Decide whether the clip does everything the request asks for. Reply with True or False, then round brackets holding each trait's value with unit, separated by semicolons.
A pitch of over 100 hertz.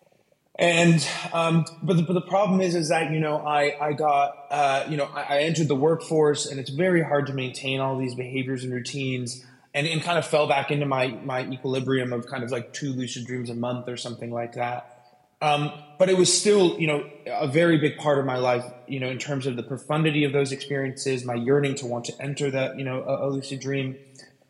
True (140 Hz)